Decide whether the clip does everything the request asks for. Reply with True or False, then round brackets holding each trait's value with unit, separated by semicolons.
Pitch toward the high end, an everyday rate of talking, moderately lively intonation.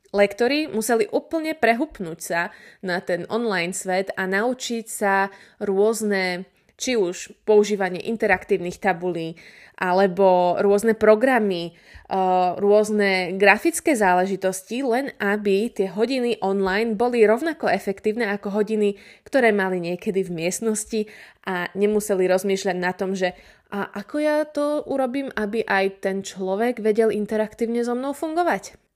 True (205 Hz; 120 wpm; 3.2 semitones)